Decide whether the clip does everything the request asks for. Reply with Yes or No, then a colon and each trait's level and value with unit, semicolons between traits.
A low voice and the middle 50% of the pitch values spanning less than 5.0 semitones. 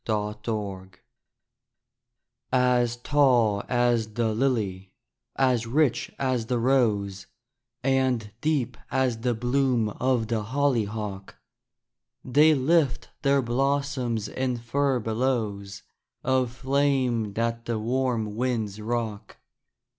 Yes: low, 120 Hz; average, 3.3 semitones